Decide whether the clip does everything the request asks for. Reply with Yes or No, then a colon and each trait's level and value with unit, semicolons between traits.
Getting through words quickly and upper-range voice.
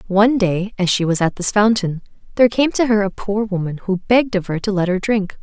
Yes: fast, 255 wpm; high, 200 Hz